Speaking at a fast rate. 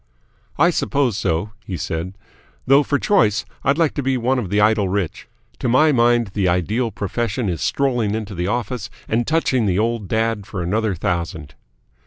No: average, 180 wpm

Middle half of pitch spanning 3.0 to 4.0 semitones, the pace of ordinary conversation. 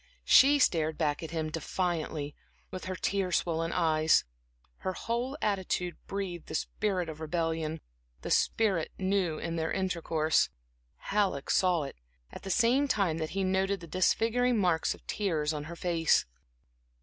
Yes: average, 3.4 semitones; average, 150 wpm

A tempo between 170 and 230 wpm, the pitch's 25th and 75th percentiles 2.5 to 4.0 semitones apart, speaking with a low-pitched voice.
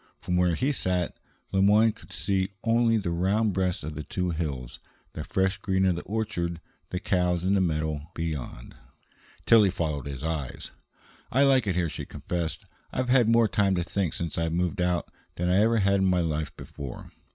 Yes: average, 195 wpm; average, 3.4 semitones; very low, 90 Hz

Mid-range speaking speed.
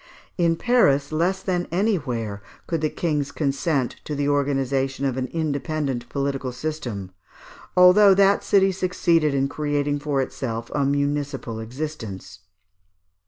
No: slow, 130 wpm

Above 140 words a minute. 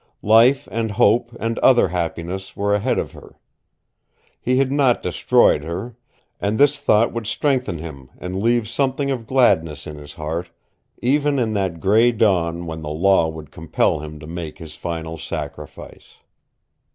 Yes: average, 160 wpm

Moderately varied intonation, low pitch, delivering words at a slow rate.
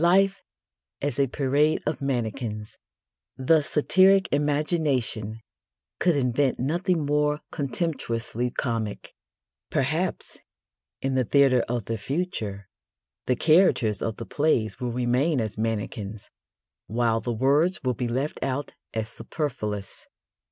Yes: average, 4.6 semitones; low, 130 Hz; slow, 115 wpm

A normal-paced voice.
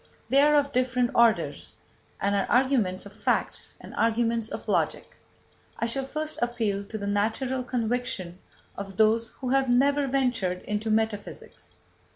Yes: average, 150 wpm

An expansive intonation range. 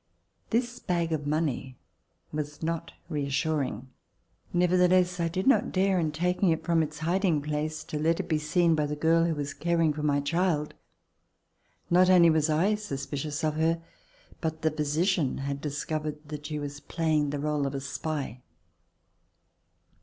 No: narrow, 2.5 semitones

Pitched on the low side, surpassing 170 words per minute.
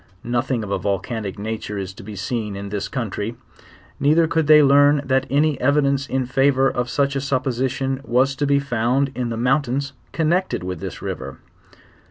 Yes: low, 130 Hz; average, 180 wpm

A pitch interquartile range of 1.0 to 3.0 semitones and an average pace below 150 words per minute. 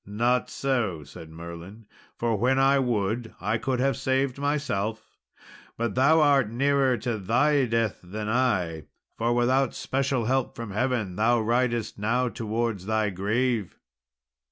No: average, 3.6 semitones; average, 140 wpm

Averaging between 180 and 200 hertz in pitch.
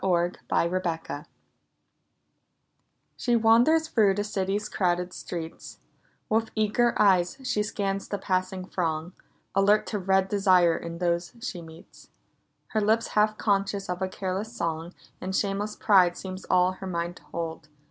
Yes: high, 190 Hz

